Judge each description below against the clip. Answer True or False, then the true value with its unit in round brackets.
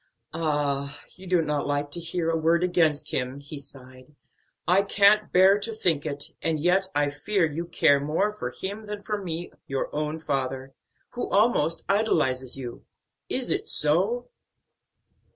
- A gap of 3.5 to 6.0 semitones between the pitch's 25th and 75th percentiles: True (5.0 semitones)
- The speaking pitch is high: False (160 Hz)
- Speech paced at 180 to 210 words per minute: False (160 wpm)